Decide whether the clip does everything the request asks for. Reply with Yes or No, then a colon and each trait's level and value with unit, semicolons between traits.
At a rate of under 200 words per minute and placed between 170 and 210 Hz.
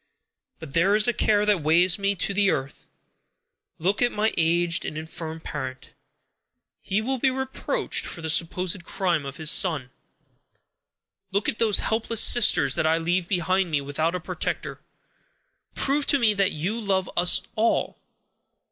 Yes: average, 160 wpm; medium, 185 Hz